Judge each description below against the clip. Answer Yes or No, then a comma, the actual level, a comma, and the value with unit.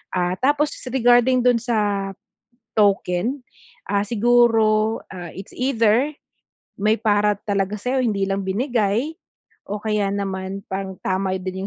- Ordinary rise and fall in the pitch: Yes, average, 3.7 semitones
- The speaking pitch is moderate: No, high, 210 Hz